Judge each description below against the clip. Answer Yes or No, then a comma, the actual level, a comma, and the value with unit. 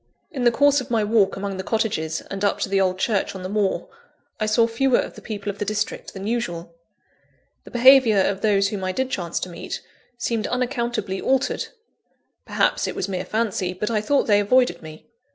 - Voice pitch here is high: Yes, high, 210 Hz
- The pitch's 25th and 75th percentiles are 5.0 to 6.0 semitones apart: No, average, 3.7 semitones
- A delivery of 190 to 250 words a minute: Yes, fast, 205 wpm